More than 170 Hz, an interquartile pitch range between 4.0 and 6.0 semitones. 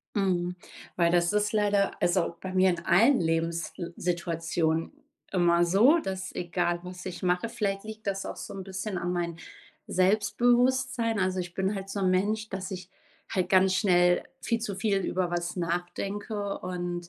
No: medium, 185 Hz; narrow, 2.6 semitones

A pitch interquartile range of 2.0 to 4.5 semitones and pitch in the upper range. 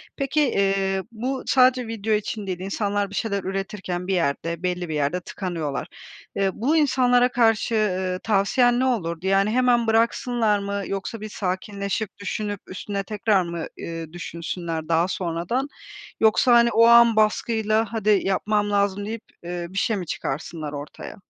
Yes: average, 3.8 semitones; high, 200 Hz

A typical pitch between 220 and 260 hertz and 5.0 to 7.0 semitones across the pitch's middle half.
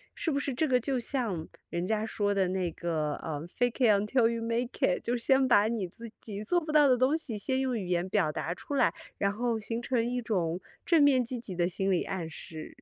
Yes: high, 225 Hz; wide, 5.6 semitones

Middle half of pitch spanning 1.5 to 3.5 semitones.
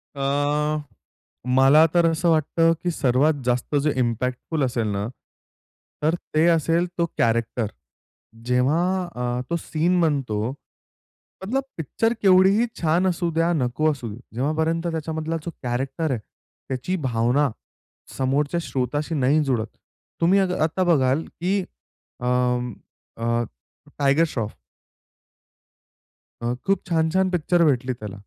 No: average, 4.9 semitones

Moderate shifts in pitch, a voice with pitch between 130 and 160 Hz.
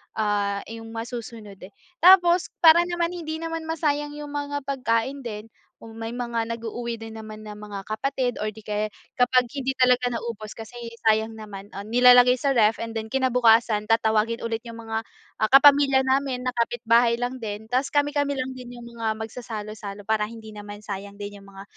No: average, 3.4 semitones; high, 230 Hz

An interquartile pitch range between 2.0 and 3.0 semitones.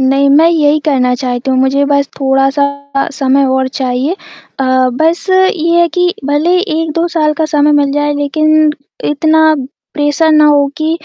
Yes: narrow, 2.4 semitones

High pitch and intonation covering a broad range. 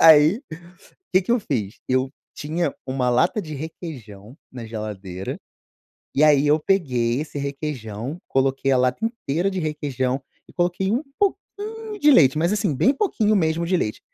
No: medium, 150 Hz; wide, 5.7 semitones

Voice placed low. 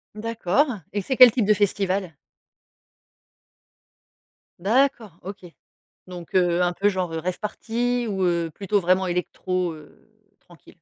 No: high, 190 Hz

